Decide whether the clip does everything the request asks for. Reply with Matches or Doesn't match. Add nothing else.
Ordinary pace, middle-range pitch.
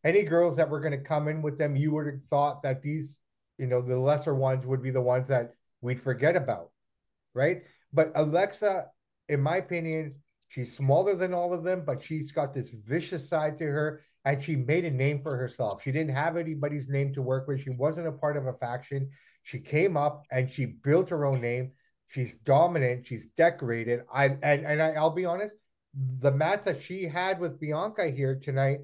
Doesn't match